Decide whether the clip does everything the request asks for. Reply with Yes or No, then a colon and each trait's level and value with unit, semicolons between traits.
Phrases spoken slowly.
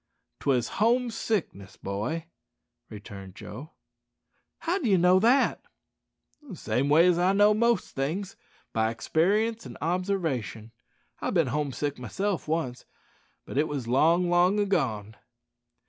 Yes: slow, 130 wpm